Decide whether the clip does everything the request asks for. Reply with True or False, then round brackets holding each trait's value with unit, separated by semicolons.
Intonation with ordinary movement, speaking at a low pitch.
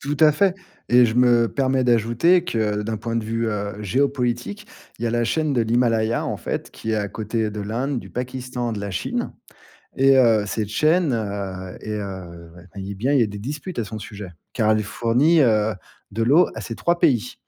True (3.7 semitones; 115 Hz)